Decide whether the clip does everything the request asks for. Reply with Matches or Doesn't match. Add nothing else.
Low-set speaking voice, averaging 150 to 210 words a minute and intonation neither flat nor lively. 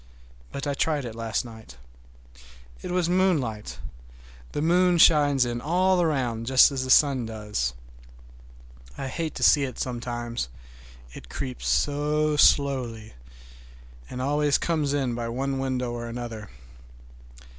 Doesn't match